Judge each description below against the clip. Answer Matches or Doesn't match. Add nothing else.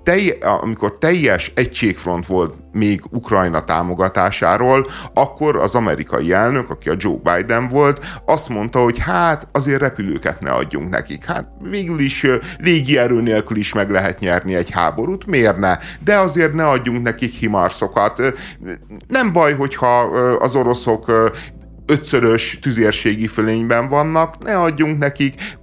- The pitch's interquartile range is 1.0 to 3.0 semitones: Doesn't match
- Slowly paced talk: Doesn't match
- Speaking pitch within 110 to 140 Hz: Matches